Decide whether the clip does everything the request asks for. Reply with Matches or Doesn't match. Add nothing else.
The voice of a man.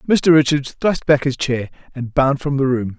Matches